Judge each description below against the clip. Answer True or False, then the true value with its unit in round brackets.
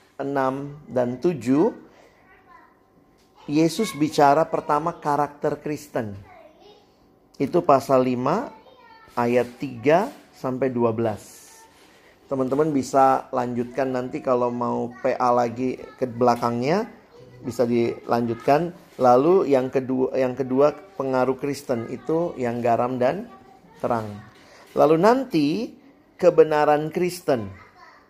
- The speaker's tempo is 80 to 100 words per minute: True (90 wpm)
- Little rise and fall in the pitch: False (3.6 semitones)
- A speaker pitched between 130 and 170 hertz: True (135 Hz)